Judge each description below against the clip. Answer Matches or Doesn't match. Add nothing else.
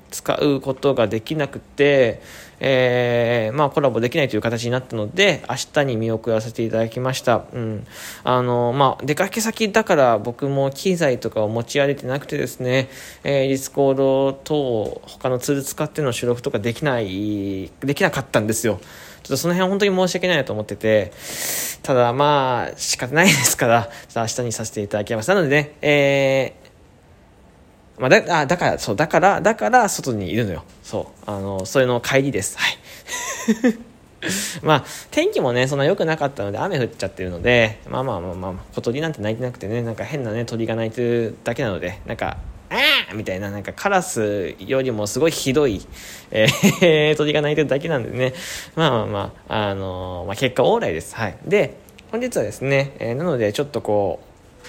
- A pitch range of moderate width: Matches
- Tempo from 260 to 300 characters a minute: Doesn't match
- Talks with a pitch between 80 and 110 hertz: Doesn't match